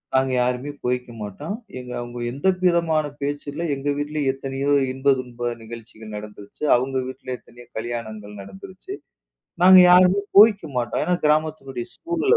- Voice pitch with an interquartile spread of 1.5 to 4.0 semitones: No, average, 4.5 semitones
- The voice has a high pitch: No, low, 135 Hz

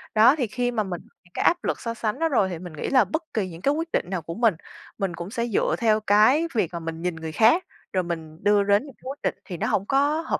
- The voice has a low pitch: No, high, 210 Hz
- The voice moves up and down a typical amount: No, wide, 6.3 semitones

